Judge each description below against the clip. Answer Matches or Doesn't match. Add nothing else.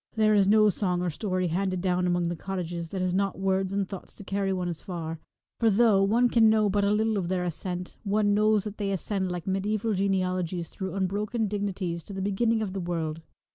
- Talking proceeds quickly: Matches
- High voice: Matches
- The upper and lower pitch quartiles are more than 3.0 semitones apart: Doesn't match